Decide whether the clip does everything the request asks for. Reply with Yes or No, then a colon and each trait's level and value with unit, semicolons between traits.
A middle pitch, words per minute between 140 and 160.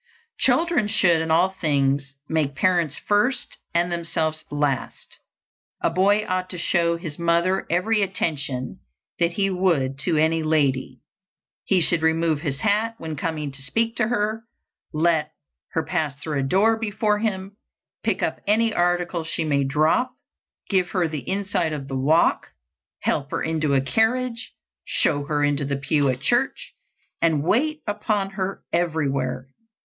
Yes: medium, 170 Hz; average, 155 wpm